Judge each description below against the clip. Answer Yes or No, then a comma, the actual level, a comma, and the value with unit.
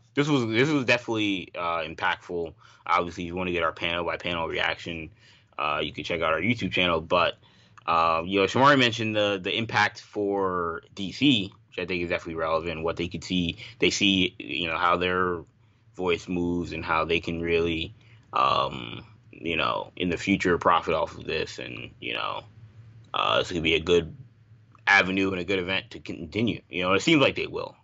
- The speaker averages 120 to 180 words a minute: No, average, 200 wpm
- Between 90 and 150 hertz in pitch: Yes, very low, 95 Hz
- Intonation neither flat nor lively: Yes, average, 4.9 semitones